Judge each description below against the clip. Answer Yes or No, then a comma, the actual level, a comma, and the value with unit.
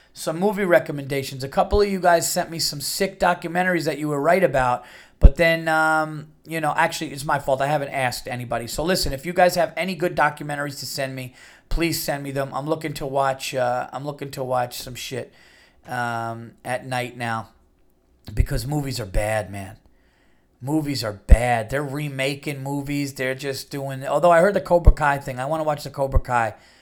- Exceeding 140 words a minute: Yes, average, 200 wpm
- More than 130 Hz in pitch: Yes, medium, 140 Hz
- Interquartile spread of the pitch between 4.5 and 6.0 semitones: No, average, 4.1 semitones